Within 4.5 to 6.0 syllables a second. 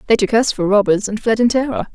No: 6.4 syllables/s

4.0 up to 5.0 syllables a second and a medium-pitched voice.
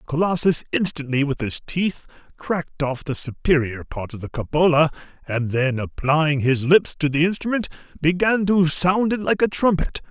Yes: 4.8 syllables/s; medium, 155 Hz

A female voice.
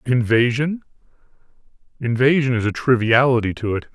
No: male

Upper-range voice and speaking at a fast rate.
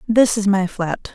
Yes: high, 200 Hz; fast, 210 wpm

